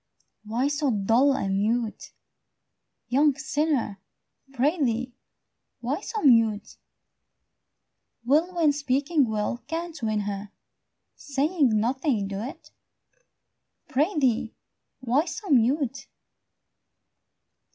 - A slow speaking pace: Yes, slow, 85 wpm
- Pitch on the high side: Yes, very high, 265 Hz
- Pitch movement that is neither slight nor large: Yes, average, 4.9 semitones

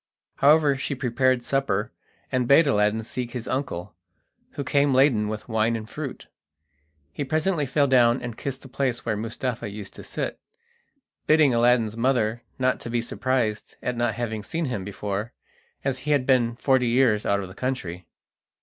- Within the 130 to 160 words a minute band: No, average, 170 wpm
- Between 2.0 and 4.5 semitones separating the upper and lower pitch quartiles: Yes, average, 3.4 semitones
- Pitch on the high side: No, low, 125 Hz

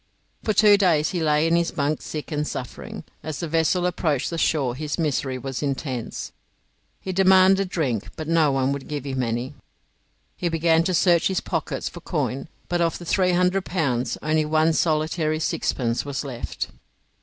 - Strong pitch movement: No, average, 3.8 semitones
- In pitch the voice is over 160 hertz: No, medium, 155 Hz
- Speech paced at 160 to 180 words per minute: Yes, average, 175 wpm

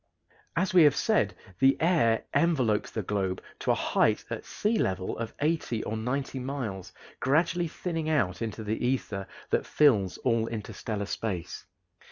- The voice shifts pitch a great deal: Yes, wide, 6.5 semitones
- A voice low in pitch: Yes, low, 115 Hz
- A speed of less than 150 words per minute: No, average, 155 wpm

